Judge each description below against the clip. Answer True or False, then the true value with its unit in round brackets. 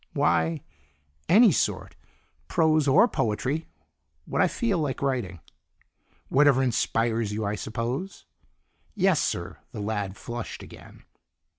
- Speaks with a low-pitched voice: True (130 Hz)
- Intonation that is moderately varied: False (6.3 semitones)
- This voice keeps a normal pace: False (115 wpm)